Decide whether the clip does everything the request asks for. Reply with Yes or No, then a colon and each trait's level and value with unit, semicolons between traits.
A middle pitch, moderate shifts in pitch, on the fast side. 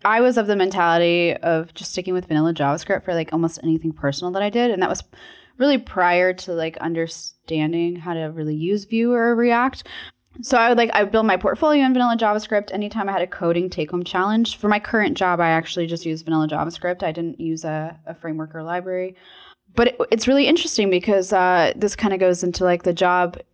Yes: medium, 180 Hz; average, 4.1 semitones; fast, 220 wpm